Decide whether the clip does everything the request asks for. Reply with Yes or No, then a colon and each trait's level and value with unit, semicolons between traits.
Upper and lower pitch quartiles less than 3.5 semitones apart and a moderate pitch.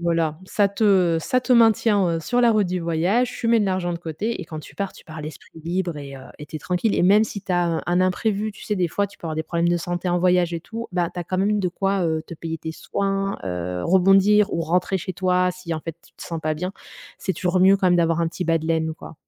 Yes: average, 3.1 semitones; medium, 180 Hz